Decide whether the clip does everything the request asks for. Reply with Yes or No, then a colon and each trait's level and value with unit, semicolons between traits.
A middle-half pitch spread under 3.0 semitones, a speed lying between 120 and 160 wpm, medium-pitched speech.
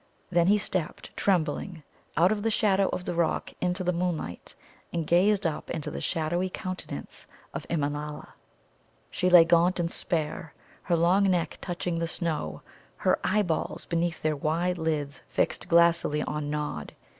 Yes: narrow, 2.5 semitones; average, 155 wpm; medium, 170 Hz